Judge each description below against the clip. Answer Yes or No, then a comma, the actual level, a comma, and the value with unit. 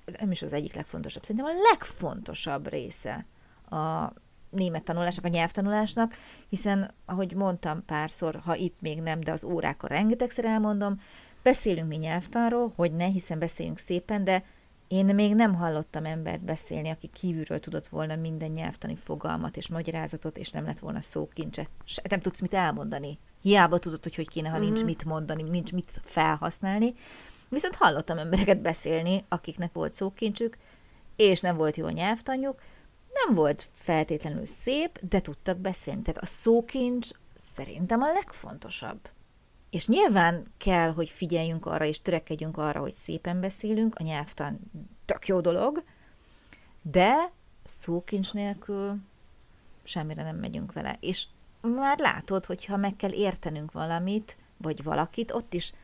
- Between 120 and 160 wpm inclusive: Yes, average, 145 wpm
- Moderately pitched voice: Yes, medium, 180 Hz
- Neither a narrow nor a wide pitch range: Yes, average, 4.2 semitones